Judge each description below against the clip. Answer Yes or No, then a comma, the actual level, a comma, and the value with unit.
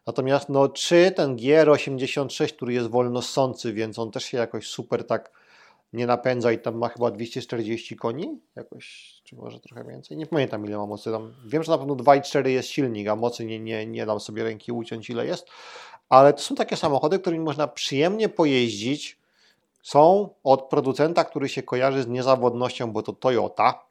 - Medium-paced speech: No, fast, 180 wpm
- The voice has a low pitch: Yes, low, 130 Hz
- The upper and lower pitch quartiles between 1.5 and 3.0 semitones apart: No, average, 3.8 semitones